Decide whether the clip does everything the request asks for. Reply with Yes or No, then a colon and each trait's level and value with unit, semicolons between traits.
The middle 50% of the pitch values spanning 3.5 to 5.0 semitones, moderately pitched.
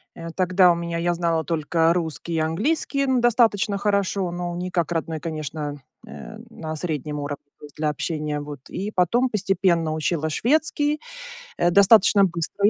Yes: average, 4.2 semitones; medium, 170 Hz